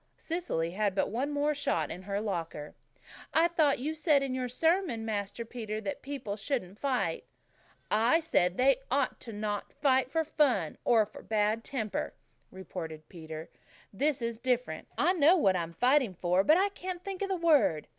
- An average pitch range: No, wide, 6.9 semitones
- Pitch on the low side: No, high, 240 Hz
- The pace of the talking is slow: No, average, 175 wpm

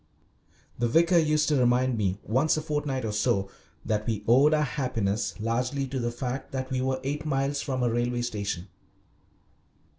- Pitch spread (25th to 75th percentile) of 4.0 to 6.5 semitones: No, average, 3.6 semitones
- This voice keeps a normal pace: Yes, average, 175 wpm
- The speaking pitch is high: No, low, 130 Hz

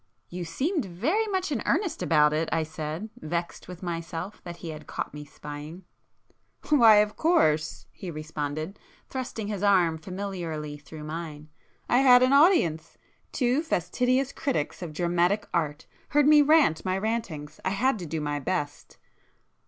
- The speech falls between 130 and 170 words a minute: Yes, average, 150 wpm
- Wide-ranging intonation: Yes, wide, 8.0 semitones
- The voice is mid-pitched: Yes, medium, 175 Hz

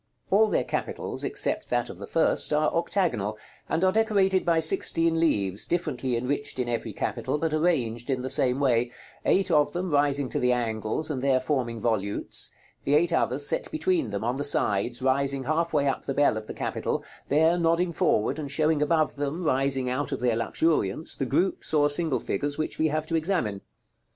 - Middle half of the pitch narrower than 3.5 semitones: No, average, 4.7 semitones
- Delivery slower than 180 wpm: No, average, 200 wpm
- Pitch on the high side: No, medium, 145 Hz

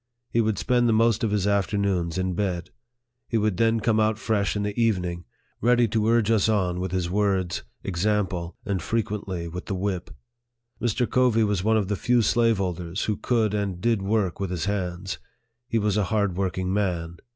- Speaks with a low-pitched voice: Yes, low, 100 Hz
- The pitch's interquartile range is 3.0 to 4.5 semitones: Yes, average, 3.3 semitones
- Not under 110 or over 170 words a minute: No, average, 195 wpm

